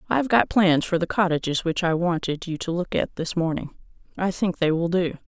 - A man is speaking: No, female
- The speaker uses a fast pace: Yes, fast, 235 wpm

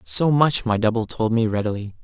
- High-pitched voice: No, low, 115 Hz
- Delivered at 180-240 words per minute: Yes, fast, 205 wpm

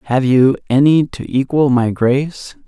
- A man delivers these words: Yes, male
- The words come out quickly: No, average, 155 wpm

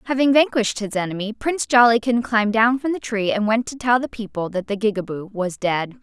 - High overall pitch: Yes, high, 220 Hz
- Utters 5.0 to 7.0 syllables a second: Yes, 5.9 syllables/s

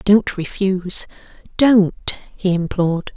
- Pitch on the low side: No, high, 190 Hz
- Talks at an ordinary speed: No, slow, 95 wpm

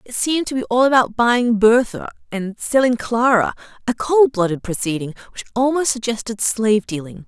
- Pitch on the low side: No, high, 230 Hz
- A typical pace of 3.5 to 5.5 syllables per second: Yes, 5.2 syllables/s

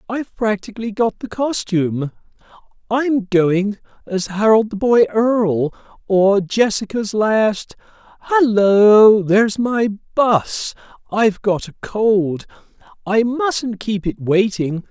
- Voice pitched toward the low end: No, high, 210 Hz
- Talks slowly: Yes, slow, 110 wpm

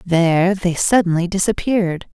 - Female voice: Yes, female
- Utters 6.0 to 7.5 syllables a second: No, 5.0 syllables/s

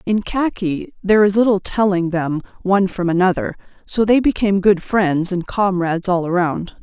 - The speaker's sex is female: Yes, female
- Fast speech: No, average, 165 wpm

